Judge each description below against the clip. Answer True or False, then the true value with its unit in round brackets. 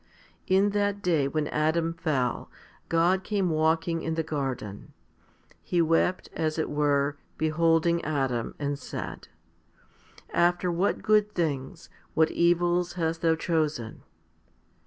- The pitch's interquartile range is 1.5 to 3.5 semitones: True (2.6 semitones)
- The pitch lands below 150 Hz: False (165 Hz)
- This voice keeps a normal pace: False (125 wpm)